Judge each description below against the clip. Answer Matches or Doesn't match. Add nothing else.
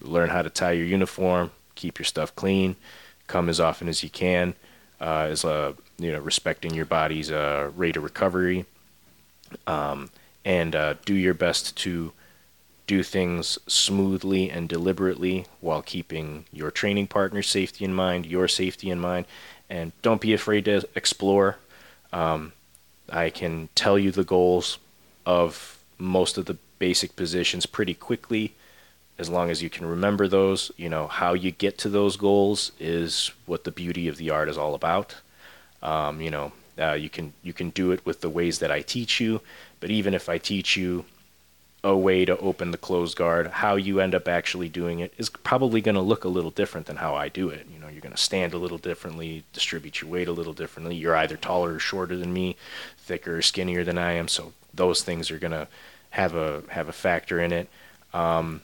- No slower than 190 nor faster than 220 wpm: Matches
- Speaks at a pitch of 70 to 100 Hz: Matches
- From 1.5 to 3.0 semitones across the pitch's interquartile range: Matches